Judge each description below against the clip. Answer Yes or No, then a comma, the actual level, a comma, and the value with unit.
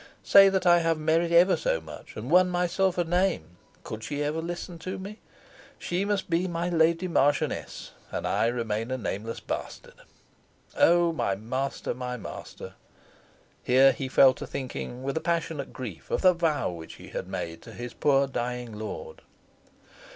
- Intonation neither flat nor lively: No, wide, 6.0 semitones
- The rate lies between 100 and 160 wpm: No, average, 170 wpm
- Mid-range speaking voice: Yes, medium, 160 Hz